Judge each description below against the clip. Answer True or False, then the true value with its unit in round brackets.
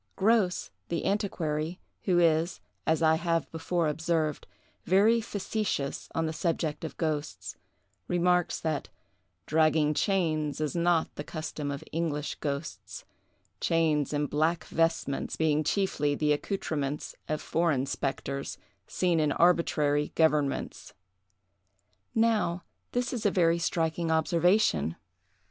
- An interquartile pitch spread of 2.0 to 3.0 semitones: True (2.6 semitones)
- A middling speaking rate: False (120 wpm)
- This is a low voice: False (160 Hz)